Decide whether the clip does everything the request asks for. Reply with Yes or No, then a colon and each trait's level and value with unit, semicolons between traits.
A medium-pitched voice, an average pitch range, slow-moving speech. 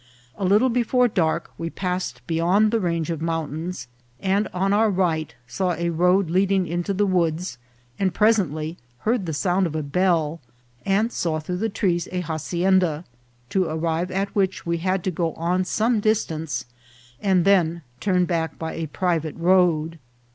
No: medium, 180 Hz; average, 3.0 semitones; average, 170 wpm